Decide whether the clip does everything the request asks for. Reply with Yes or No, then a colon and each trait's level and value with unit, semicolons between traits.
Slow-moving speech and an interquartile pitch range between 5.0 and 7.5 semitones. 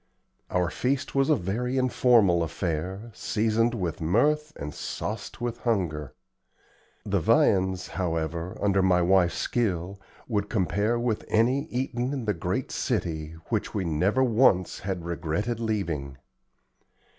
Yes: slow, 130 wpm; wide, 5.5 semitones